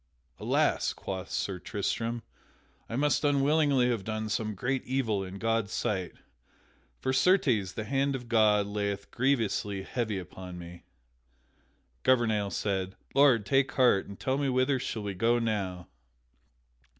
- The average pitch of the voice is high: No, low, 110 Hz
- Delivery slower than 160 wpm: Yes, average, 140 wpm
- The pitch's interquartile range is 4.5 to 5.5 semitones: Yes, average, 4.8 semitones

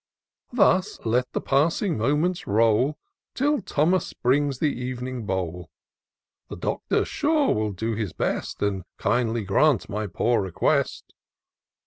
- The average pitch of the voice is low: Yes, low, 125 Hz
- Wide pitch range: Yes, wide, 6.2 semitones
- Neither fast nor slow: No, slow, 125 wpm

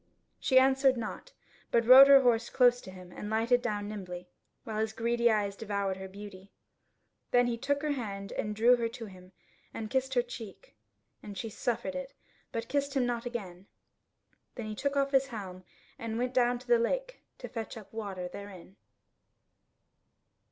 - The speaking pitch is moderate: No, high, 230 Hz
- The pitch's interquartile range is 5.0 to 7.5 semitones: No, average, 3.7 semitones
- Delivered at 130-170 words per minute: No, average, 180 wpm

